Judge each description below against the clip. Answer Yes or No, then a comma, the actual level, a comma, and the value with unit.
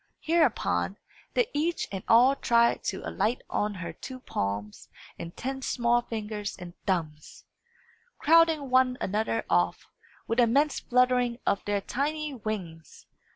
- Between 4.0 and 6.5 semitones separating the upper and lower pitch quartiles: Yes, wide, 5.6 semitones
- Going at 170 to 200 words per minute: No, slow, 135 wpm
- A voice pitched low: No, high, 235 Hz